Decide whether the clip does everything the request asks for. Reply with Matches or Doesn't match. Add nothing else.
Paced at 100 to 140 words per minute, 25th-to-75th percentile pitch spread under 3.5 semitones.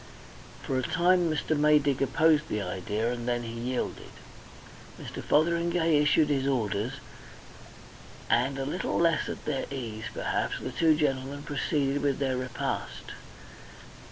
Doesn't match